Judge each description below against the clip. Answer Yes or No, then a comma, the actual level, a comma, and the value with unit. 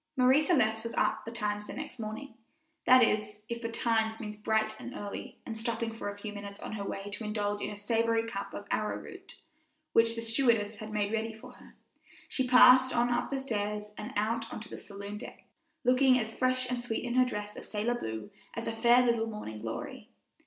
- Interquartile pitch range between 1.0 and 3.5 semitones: Yes, narrow, 2.4 semitones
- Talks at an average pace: No, fast, 210 wpm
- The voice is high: Yes, high, 225 Hz